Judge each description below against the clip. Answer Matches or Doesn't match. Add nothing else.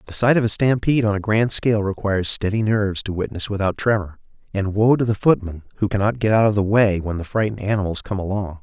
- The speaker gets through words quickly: Matches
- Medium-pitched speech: Doesn't match